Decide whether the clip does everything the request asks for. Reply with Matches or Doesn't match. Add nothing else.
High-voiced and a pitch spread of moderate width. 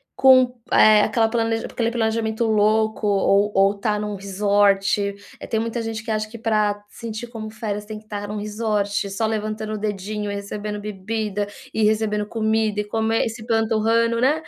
Doesn't match